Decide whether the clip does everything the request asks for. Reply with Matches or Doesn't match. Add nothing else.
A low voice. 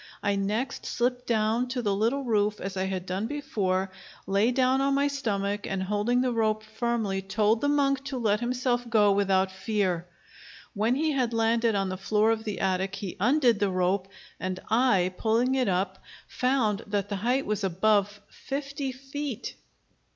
Doesn't match